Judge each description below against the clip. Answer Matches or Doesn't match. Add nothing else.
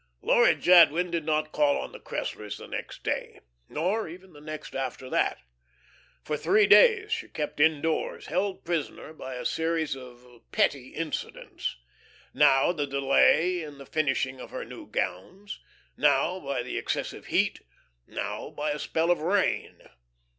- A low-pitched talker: Doesn't match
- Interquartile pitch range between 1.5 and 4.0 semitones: Doesn't match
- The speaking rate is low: Doesn't match